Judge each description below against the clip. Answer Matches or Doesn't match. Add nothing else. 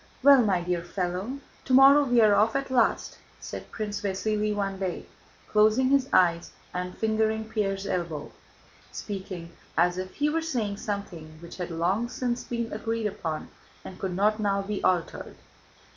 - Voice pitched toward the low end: Doesn't match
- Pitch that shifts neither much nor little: Matches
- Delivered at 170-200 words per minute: Doesn't match